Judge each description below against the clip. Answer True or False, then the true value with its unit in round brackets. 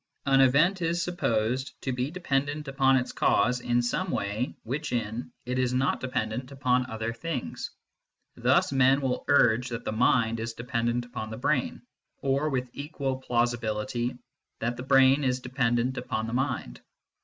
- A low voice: True (125 Hz)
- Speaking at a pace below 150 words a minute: False (160 wpm)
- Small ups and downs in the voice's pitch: True (2.3 semitones)